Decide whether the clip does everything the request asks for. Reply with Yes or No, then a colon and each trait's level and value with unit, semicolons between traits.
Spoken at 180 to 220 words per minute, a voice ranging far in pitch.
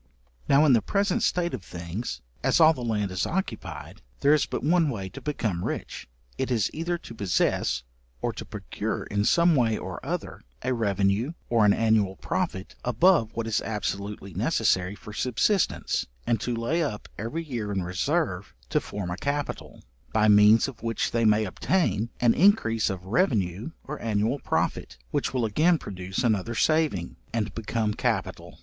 No: average, 170 wpm; wide, 5.9 semitones